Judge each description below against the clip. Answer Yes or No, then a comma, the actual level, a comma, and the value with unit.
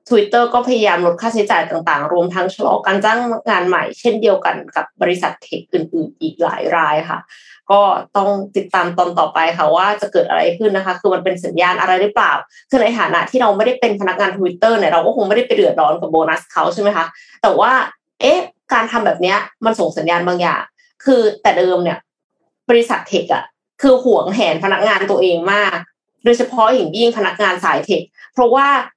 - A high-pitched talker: Yes, high, 205 Hz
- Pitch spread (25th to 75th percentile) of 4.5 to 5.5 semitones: Yes, average, 4.8 semitones